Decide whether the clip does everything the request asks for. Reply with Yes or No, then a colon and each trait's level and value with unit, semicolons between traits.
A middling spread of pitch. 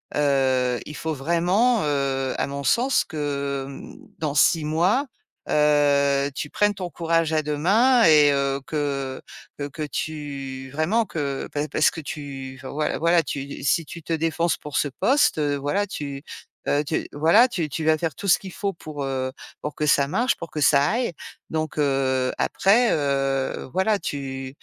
Yes: average, 3.2 semitones